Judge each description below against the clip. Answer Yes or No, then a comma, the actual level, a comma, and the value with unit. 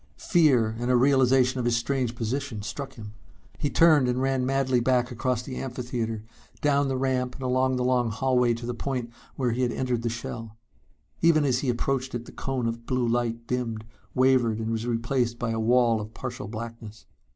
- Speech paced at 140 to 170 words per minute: No, average, 195 wpm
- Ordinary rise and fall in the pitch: No, narrow, 2.1 semitones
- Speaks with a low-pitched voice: Yes, low, 125 Hz